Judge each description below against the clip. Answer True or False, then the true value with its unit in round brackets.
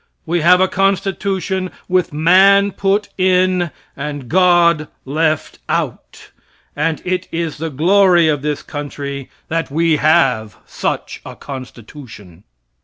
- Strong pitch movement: False (4.0 semitones)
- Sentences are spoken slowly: True (120 wpm)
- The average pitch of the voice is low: False (165 Hz)